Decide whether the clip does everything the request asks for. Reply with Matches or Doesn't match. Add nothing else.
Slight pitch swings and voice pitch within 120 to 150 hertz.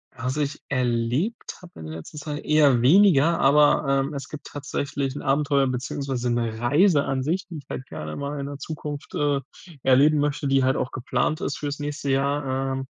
Matches